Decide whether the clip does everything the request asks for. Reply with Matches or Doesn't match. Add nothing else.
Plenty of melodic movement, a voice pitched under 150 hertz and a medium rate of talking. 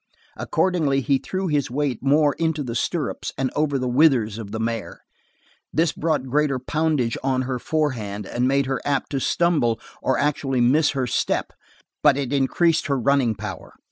Doesn't match